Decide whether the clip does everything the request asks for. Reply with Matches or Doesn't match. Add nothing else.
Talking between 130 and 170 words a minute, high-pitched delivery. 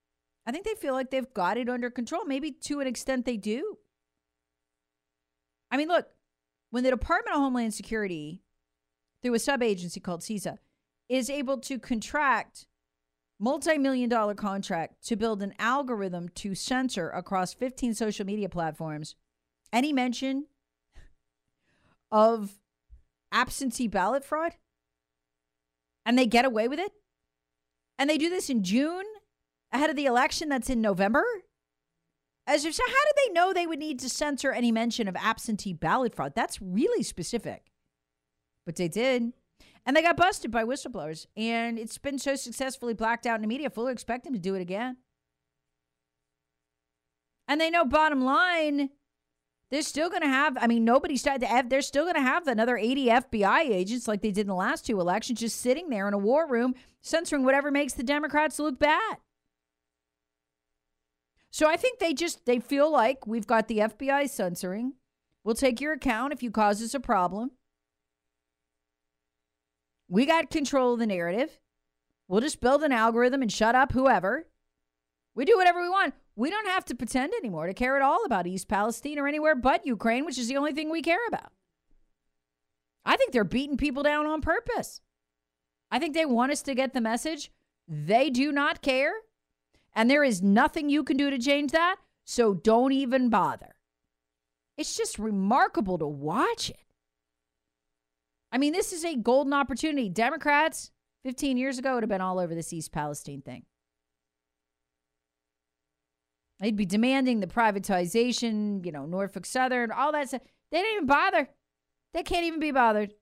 Matches